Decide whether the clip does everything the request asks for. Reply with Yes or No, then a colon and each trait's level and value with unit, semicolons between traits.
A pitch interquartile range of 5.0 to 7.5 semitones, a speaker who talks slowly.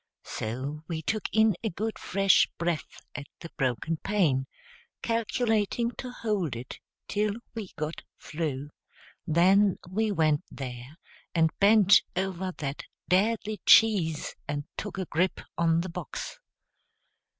Yes: wide, 5.4 semitones; slow, 130 wpm